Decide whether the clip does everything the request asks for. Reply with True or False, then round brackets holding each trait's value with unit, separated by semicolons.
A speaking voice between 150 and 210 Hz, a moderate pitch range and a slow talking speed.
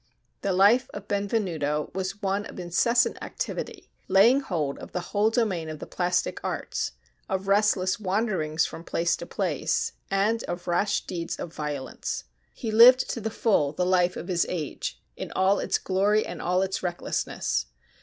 False (190 Hz; 3.2 semitones; 165 wpm)